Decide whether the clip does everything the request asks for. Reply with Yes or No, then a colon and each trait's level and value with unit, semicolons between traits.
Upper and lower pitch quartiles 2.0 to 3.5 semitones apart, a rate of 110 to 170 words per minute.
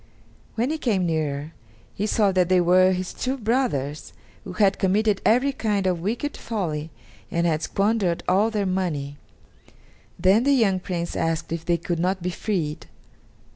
No: average, 4.2 semitones; average, 165 wpm